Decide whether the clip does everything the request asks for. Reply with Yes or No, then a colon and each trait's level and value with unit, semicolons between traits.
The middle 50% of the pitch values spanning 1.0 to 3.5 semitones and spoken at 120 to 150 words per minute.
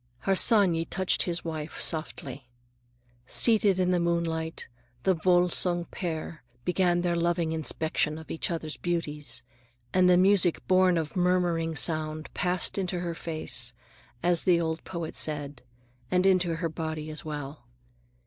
Yes: narrow, 2.4 semitones; average, 140 wpm